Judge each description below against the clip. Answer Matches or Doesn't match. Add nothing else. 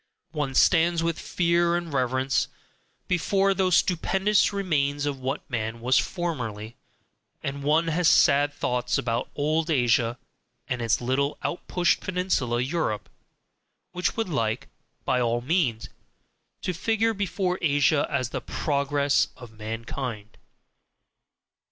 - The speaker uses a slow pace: Matches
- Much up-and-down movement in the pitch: Matches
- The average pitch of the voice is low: Doesn't match